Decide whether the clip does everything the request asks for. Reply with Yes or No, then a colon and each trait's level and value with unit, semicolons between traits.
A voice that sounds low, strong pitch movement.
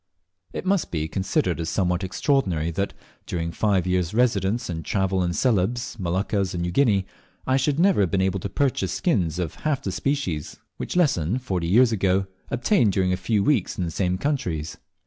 Yes: very low, 95 Hz; wide, 5.7 semitones